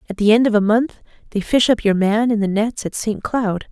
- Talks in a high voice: Yes, high, 215 Hz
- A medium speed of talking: No, fast, 275 wpm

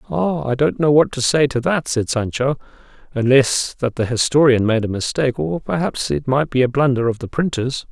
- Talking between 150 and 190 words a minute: No, fast, 205 wpm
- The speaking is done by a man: Yes, male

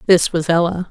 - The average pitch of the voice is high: No, medium, 170 Hz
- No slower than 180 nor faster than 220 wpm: Yes, average, 200 wpm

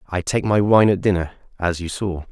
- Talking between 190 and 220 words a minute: No, fast, 235 wpm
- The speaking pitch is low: Yes, very low, 95 Hz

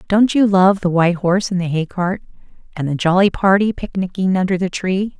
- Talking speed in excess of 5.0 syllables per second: Yes, 5.6 syllables/s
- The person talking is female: Yes, female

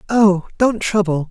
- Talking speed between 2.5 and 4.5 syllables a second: Yes, 3.9 syllables/s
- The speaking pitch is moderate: No, high, 195 Hz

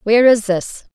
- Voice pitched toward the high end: Yes, high, 215 Hz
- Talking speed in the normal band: Yes, average, 190 wpm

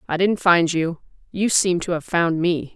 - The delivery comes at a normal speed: No, fast, 220 wpm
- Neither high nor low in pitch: Yes, medium, 175 Hz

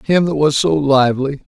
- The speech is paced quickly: No, average, 195 wpm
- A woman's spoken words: No, male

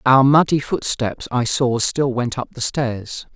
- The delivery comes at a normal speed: Yes, average, 180 wpm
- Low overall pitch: Yes, low, 125 Hz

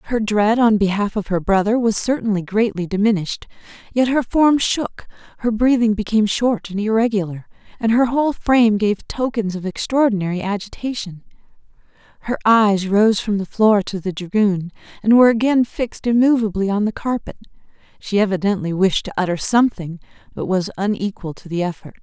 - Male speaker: No, female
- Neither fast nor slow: Yes, average, 160 wpm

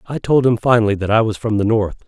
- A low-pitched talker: Yes, low, 110 Hz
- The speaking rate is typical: No, fast, 290 wpm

